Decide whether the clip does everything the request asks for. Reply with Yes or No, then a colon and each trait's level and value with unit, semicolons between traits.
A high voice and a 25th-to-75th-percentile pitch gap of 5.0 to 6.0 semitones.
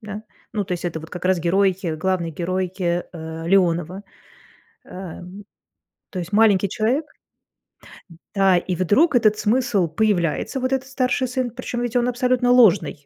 Yes: high, 195 Hz; wide, 5.5 semitones